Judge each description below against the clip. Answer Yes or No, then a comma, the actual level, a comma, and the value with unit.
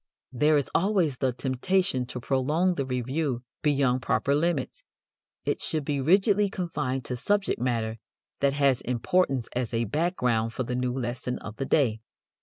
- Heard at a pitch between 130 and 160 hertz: Yes, low, 135 Hz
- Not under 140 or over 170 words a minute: Yes, average, 160 wpm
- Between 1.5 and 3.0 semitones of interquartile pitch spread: No, average, 4.0 semitones